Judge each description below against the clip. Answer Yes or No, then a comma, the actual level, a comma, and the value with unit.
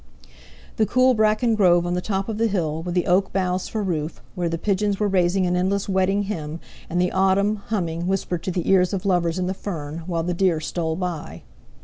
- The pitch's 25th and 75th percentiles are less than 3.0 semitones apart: Yes, narrow, 2.4 semitones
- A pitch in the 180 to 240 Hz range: Yes, medium, 185 Hz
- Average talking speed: No, fast, 220 wpm